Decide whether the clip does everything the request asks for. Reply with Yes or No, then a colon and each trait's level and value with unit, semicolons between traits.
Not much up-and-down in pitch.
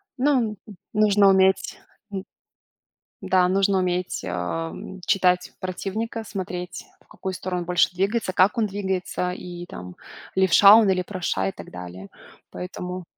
Yes: narrow, 2.0 semitones